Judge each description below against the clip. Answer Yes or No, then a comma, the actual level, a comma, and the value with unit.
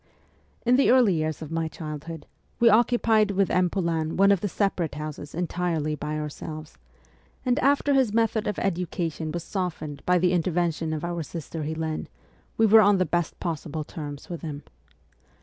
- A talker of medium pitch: Yes, medium, 170 Hz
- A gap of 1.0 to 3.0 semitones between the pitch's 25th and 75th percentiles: No, average, 4.2 semitones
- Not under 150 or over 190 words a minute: Yes, average, 175 wpm